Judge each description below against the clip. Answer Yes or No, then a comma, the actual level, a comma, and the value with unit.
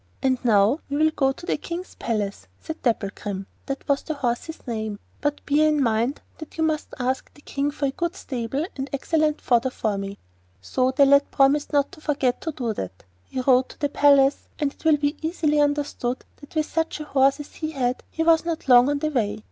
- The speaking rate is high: Yes, fast, 215 wpm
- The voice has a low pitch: No, very high, 280 Hz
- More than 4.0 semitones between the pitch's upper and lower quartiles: No, average, 3.6 semitones